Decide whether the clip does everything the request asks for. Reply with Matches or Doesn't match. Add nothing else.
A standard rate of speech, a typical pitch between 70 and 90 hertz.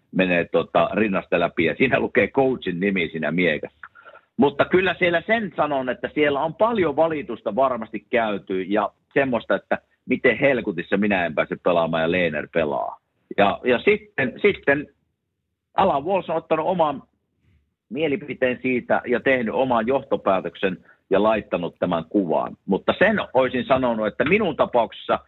Doesn't match